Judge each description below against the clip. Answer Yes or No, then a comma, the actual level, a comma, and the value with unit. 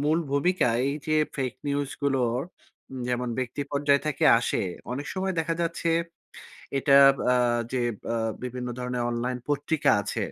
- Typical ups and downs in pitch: Yes, average, 3.2 semitones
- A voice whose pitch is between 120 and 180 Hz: Yes, medium, 140 Hz